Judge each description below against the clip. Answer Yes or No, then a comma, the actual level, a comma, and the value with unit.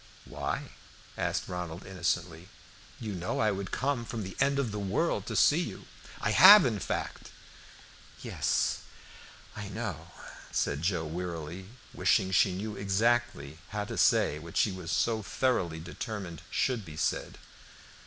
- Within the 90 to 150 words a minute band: Yes, average, 145 wpm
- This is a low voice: Yes, very low, 95 Hz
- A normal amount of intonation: Yes, average, 4.5 semitones